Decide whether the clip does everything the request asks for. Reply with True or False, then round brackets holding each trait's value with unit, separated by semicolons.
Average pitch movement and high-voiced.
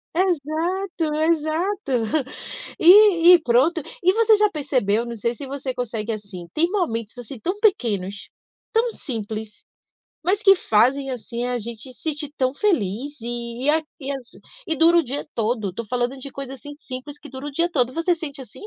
False (5.9 semitones; 275 Hz)